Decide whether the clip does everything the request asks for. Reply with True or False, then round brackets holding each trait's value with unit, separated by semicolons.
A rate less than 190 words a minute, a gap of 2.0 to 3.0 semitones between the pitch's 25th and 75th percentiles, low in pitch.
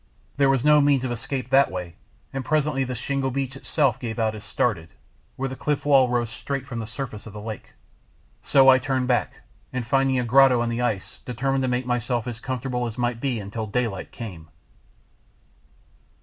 False (195 wpm; 2.7 semitones; 125 Hz)